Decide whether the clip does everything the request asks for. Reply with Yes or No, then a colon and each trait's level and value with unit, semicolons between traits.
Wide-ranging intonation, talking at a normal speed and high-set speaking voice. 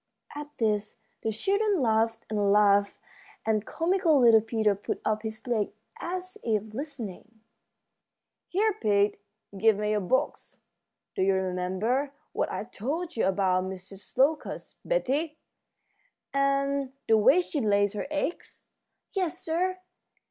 No: wide, 6.2 semitones; slow, 130 wpm; high, 225 Hz